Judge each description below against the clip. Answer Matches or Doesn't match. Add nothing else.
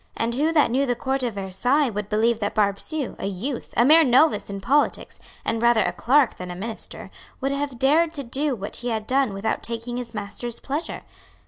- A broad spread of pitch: Doesn't match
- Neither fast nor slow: Doesn't match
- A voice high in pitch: Matches